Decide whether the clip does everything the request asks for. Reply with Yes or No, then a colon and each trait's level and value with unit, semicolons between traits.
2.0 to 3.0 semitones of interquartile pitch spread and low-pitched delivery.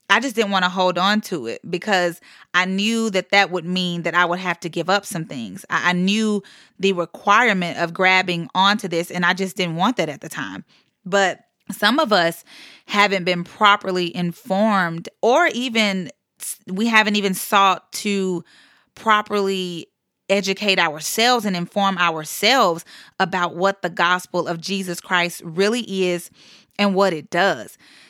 No: average, 2.7 semitones; high, 190 Hz